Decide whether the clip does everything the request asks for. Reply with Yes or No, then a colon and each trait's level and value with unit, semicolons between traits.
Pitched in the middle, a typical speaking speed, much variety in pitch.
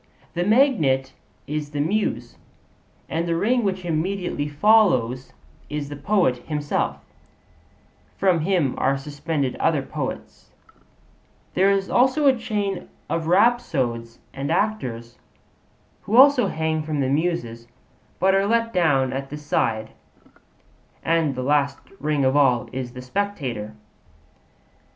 No: medium, 155 Hz; slow, 125 wpm; wide, 6.5 semitones